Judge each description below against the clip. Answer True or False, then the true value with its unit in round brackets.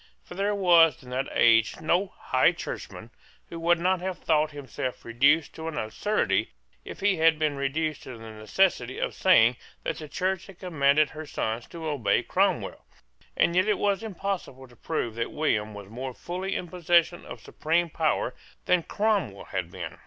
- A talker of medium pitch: True (155 Hz)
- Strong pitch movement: True (6.0 semitones)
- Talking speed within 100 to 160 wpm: False (180 wpm)